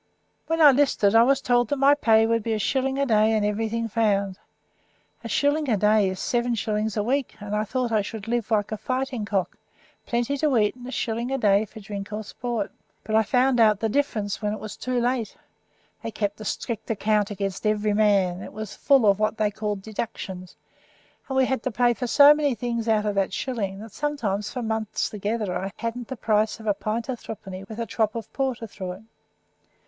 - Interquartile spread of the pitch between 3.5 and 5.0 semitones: No, average, 2.8 semitones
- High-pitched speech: Yes, high, 220 Hz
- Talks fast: Yes, fast, 220 wpm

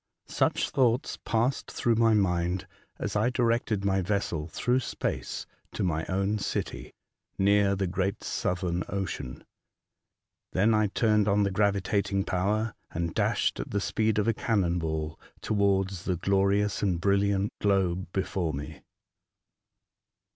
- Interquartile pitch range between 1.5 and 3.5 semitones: Yes, narrow, 2.5 semitones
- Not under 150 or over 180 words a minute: No, slow, 135 wpm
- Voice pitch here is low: Yes, low, 100 Hz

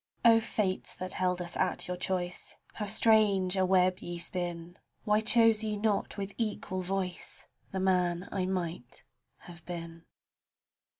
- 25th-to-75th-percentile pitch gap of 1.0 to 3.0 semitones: Yes, average, 2.7 semitones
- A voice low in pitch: No, medium, 185 Hz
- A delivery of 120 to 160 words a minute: Yes, average, 155 wpm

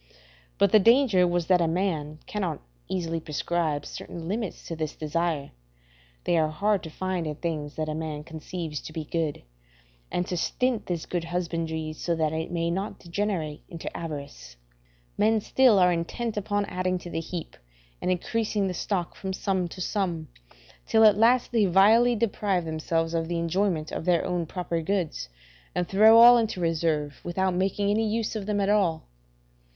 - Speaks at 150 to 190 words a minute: Yes, average, 175 wpm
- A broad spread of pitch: No, average, 3.9 semitones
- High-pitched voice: No, medium, 175 Hz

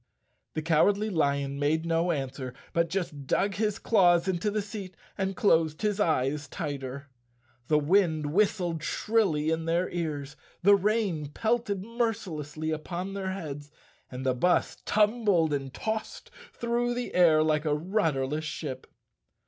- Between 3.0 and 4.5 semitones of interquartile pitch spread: No, average, 5.2 semitones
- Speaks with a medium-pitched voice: Yes, medium, 170 Hz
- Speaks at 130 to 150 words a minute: Yes, average, 140 wpm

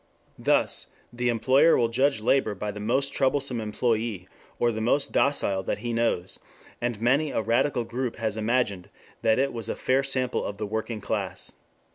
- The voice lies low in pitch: Yes, low, 115 Hz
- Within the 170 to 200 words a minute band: Yes, average, 175 wpm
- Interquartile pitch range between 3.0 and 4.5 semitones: Yes, average, 3.3 semitones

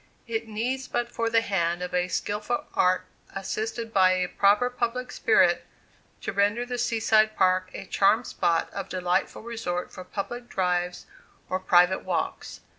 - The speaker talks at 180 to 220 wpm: No, average, 150 wpm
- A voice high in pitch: Yes, high, 200 Hz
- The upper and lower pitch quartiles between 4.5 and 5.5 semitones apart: No, average, 4.0 semitones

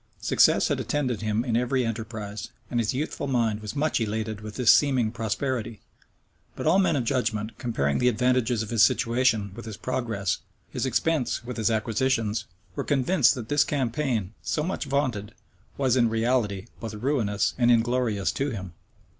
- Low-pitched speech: Yes, low, 115 Hz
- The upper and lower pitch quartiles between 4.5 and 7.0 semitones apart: No, average, 3.1 semitones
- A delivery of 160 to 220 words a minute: Yes, average, 170 wpm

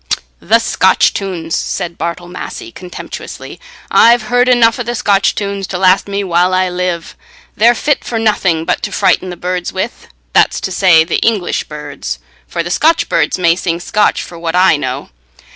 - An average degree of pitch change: Yes, average, 3.6 semitones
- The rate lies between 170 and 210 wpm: Yes, average, 175 wpm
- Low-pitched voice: No, medium, 185 Hz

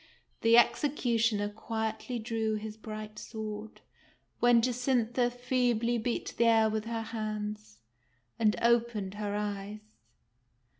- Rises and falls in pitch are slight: Yes, narrow, 1.9 semitones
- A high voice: Yes, high, 220 Hz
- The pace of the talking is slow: Yes, slow, 110 wpm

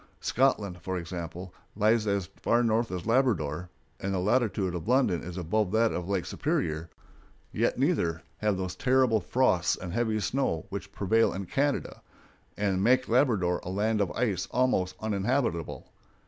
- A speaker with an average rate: Yes, average, 155 wpm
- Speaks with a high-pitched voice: No, low, 100 Hz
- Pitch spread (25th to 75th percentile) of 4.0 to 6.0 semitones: Yes, average, 4.6 semitones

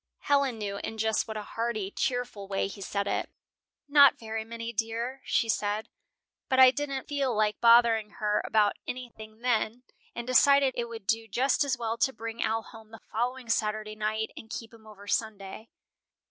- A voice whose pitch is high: Yes, high, 225 Hz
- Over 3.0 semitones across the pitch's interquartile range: No, narrow, 2.5 semitones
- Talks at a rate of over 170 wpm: Yes, average, 185 wpm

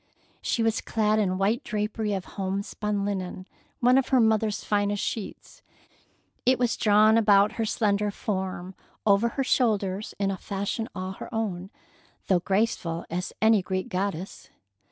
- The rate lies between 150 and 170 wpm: Yes, average, 155 wpm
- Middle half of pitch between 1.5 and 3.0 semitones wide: Yes, narrow, 2.5 semitones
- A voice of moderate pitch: No, high, 205 Hz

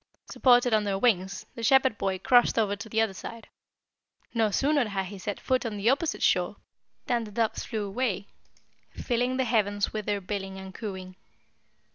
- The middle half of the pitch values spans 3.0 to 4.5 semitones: Yes, average, 3.6 semitones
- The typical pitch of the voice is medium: No, high, 215 Hz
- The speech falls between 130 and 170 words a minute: No, average, 180 wpm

